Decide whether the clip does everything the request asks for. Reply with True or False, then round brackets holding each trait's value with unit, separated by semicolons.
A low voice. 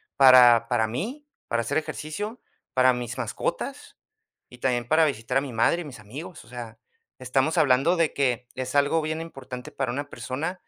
True (130 Hz)